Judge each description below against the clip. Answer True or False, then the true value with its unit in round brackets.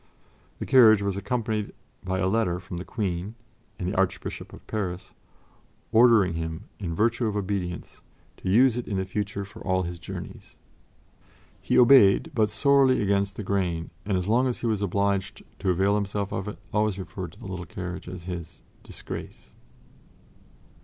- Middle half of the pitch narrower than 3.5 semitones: True (2.9 semitones)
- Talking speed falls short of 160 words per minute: False (170 wpm)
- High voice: False (100 Hz)